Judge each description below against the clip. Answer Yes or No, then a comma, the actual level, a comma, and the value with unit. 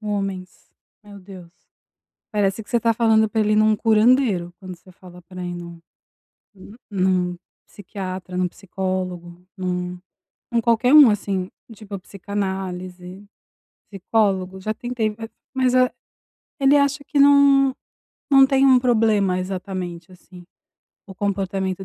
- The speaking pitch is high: Yes, high, 195 Hz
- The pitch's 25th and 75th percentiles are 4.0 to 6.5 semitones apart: No, average, 3.6 semitones